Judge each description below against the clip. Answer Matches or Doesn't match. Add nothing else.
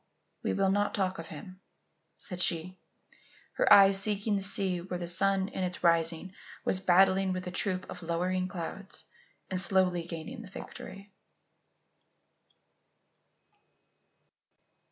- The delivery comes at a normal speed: Doesn't match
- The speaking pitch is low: Doesn't match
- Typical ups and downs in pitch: Doesn't match